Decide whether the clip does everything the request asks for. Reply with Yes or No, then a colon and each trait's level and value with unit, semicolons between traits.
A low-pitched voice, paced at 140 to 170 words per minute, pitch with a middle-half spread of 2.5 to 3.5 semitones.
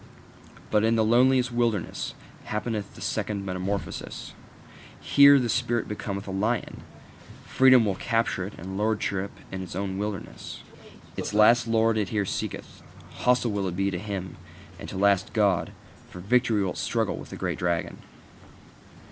Yes: low, 105 Hz; average, 160 wpm; average, 3.1 semitones